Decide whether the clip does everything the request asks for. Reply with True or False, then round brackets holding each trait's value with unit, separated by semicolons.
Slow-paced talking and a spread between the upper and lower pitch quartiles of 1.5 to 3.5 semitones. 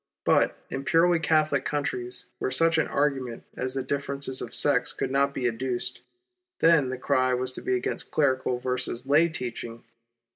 False (170 wpm; 2.4 semitones)